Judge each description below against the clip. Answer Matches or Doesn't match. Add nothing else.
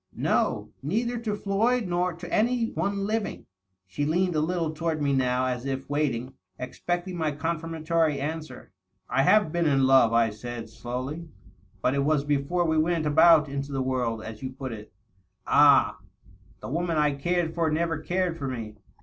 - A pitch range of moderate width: Matches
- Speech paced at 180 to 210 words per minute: Matches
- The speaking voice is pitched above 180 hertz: Doesn't match